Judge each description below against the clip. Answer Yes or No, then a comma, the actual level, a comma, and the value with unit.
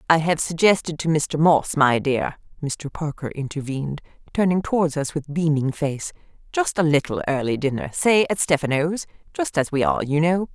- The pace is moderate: Yes, average, 165 wpm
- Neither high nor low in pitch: Yes, medium, 150 Hz